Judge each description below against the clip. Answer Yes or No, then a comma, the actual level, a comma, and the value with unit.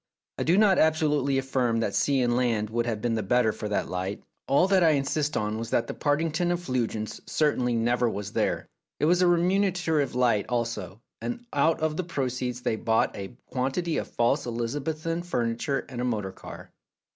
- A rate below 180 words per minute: No, average, 190 wpm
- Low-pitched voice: Yes, low, 125 Hz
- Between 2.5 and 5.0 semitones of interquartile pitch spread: No, wide, 5.4 semitones